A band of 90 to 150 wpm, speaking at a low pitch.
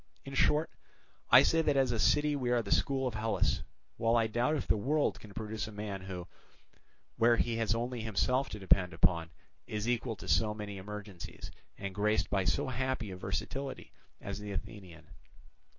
No: average, 185 wpm; low, 110 Hz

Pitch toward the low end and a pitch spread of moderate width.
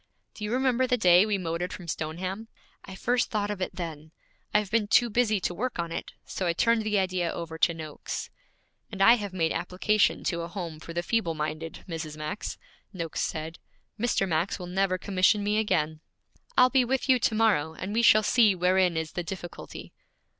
No: medium, 185 Hz; average, 4.3 semitones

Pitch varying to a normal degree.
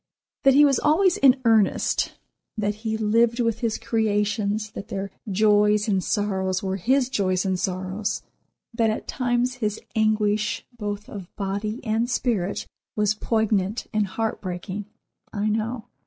No: narrow, 2.3 semitones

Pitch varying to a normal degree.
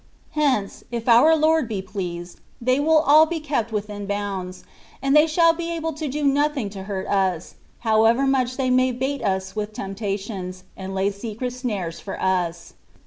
No: wide, 6.5 semitones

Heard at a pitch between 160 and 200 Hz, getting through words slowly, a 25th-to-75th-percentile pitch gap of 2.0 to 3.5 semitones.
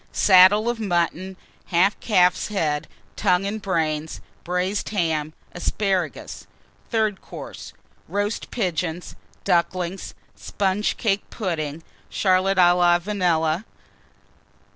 Yes: medium, 185 Hz; slow, 100 wpm; average, 2.8 semitones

